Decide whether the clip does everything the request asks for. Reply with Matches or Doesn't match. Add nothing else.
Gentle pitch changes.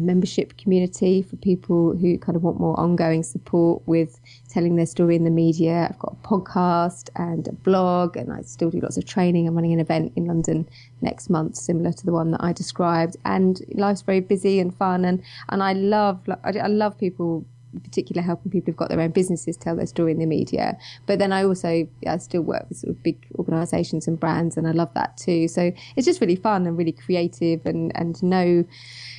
Matches